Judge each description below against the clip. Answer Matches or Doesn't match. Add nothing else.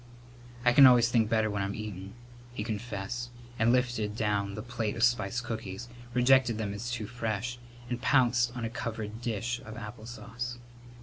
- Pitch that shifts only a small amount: Matches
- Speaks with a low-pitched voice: Matches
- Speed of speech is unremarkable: Matches